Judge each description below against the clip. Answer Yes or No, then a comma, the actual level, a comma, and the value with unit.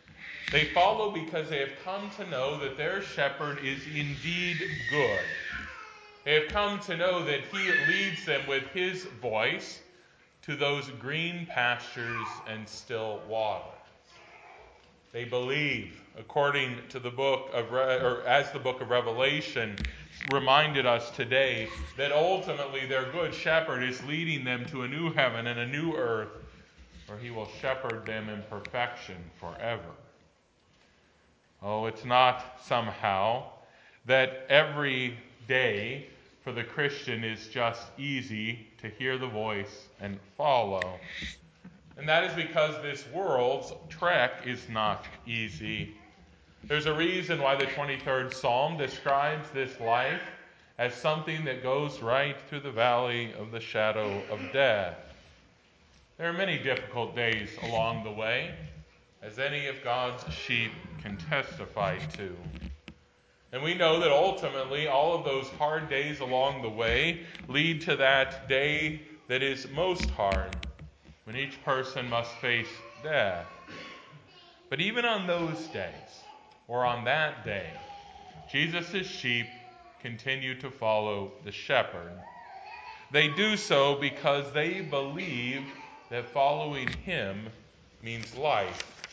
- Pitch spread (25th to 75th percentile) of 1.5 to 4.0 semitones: No, average, 4.6 semitones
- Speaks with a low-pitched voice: Yes, low, 130 Hz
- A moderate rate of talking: No, slow, 130 wpm